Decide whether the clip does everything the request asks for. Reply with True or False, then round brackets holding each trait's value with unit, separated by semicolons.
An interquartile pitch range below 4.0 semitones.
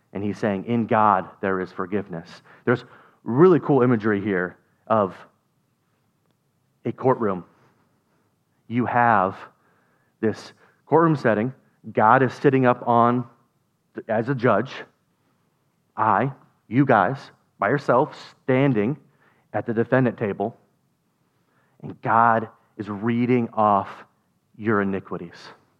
True (3.6 semitones)